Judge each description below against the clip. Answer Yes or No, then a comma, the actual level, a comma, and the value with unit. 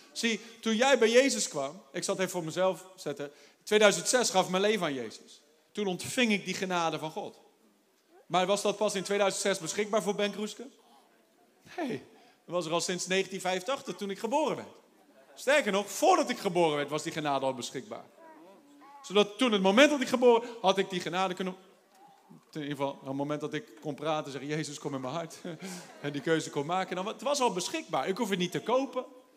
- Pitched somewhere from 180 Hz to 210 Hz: Yes, high, 190 Hz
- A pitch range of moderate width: No, wide, 6.1 semitones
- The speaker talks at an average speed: No, fast, 210 wpm